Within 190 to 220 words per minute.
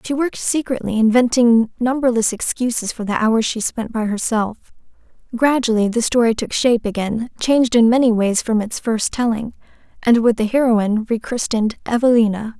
No: average, 155 wpm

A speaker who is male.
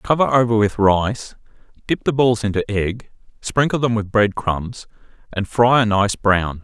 Yes: male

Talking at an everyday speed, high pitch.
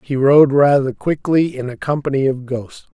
No: average, 185 wpm; low, 135 Hz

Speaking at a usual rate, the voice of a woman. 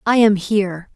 Yes: average, 190 wpm; female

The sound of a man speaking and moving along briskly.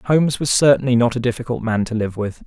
Yes: male; fast, 245 wpm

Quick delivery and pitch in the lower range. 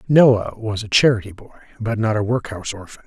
No: average, 195 wpm; low, 110 Hz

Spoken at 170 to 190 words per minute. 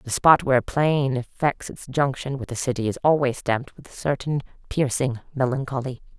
Yes: average, 185 wpm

